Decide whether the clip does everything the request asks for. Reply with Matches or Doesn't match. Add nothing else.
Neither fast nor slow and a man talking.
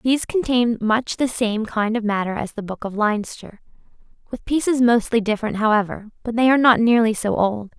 Doesn't match